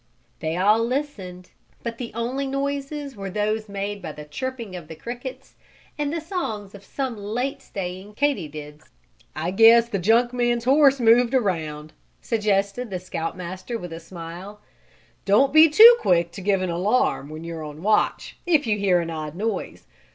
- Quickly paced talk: No, average, 175 wpm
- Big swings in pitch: Yes, wide, 5.7 semitones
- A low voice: No, high, 210 Hz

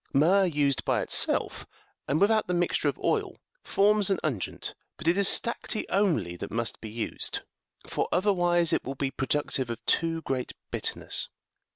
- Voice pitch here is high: No, medium, 165 Hz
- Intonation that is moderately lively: No, wide, 6.5 semitones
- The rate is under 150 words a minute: No, average, 170 wpm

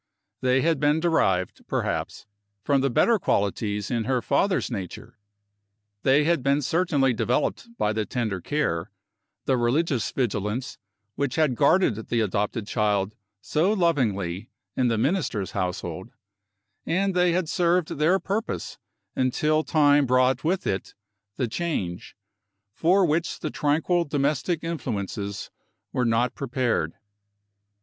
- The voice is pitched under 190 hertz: Yes, low, 135 Hz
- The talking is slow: Yes, slow, 125 wpm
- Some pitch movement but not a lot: No, wide, 6.9 semitones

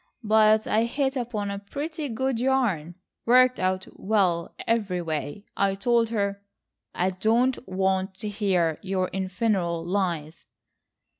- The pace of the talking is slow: Yes, slow, 120 wpm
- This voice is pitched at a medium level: No, high, 200 Hz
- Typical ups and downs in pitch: Yes, average, 3.8 semitones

